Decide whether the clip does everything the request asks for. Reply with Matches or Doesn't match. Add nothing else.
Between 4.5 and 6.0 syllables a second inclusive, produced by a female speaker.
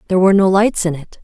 Doesn't match